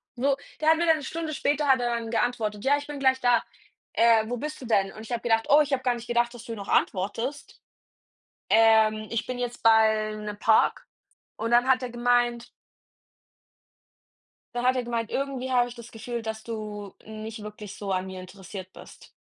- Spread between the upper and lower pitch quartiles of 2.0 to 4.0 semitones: Yes, average, 2.8 semitones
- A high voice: Yes, high, 235 Hz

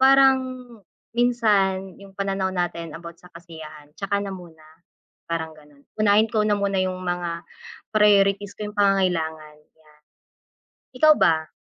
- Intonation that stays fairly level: No, average, 3.6 semitones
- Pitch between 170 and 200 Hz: Yes, high, 190 Hz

